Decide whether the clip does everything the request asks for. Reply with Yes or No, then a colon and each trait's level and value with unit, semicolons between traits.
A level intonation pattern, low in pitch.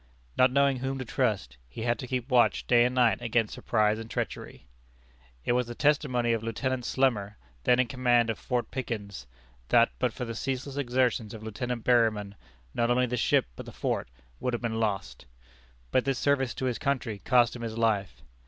Yes: narrow, 2.3 semitones; low, 120 Hz